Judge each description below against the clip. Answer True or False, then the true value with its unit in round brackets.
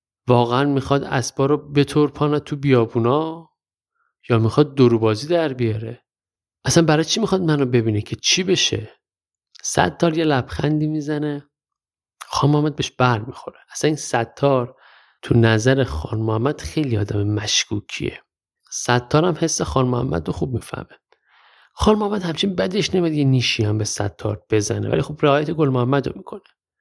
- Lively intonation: False (4.6 semitones)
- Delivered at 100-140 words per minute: False (155 wpm)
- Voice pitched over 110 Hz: True (135 Hz)